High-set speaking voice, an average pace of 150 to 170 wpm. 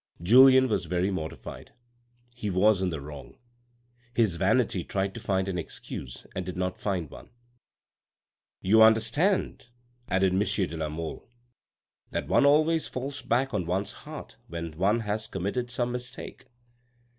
No: low, 100 Hz; average, 155 wpm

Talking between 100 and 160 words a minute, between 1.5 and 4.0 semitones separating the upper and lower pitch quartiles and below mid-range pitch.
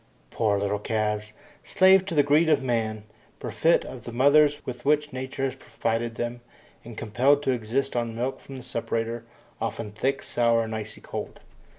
No: average, 175 wpm; average, 3.5 semitones; low, 120 Hz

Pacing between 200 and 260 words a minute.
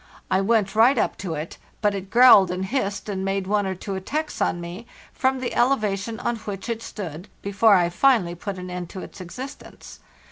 Yes: fast, 205 wpm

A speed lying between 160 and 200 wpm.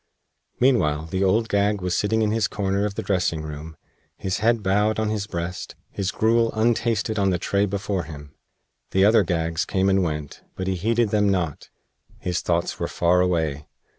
Yes: average, 185 wpm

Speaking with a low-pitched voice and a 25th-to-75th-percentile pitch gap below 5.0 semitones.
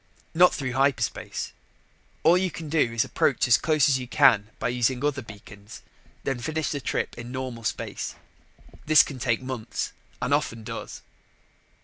Yes: low, 130 Hz; average, 4.1 semitones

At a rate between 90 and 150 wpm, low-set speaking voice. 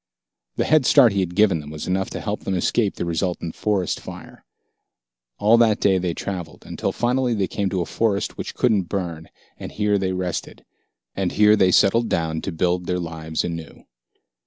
No: average, 190 wpm; very low, 95 Hz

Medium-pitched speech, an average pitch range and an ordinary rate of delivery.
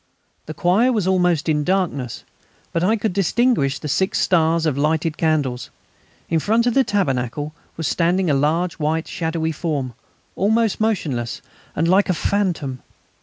Yes: medium, 165 Hz; average, 4.3 semitones; average, 160 wpm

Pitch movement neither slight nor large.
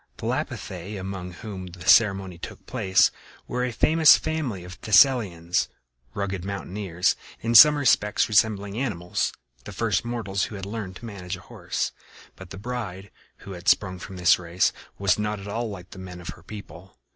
Yes: average, 3.0 semitones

